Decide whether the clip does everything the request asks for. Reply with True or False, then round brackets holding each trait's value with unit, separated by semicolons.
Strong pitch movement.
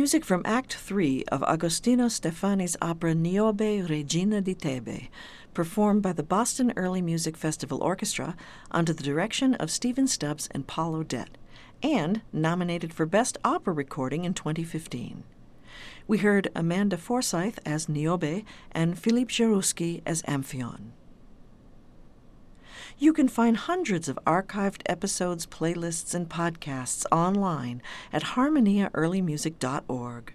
False (4.7 semitones)